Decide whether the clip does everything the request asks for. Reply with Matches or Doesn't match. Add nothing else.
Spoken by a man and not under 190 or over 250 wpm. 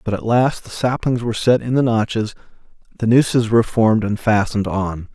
Matches